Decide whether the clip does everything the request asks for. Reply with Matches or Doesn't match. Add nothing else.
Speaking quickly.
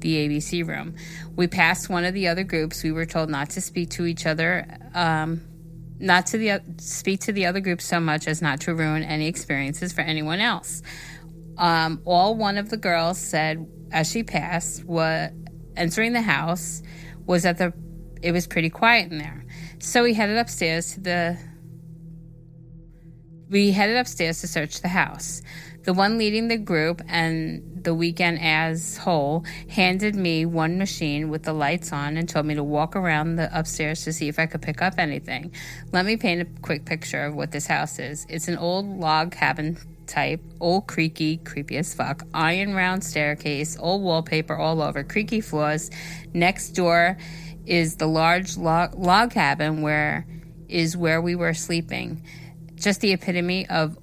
Doesn't match